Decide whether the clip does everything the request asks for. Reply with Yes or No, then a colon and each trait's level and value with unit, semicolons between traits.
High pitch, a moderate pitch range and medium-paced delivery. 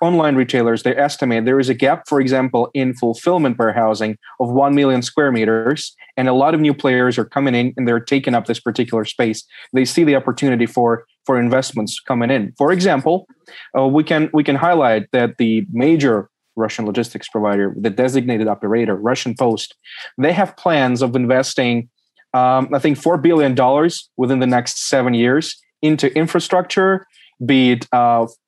No: low, 130 Hz; average, 3.1 semitones; average, 175 wpm